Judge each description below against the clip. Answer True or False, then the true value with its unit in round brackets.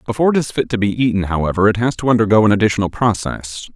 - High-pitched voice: False (110 Hz)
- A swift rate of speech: True (240 wpm)